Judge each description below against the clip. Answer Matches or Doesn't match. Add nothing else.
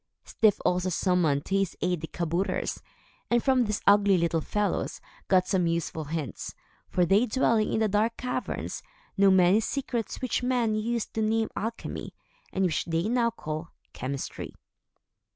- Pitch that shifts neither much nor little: Matches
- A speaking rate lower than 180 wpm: Matches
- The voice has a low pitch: Doesn't match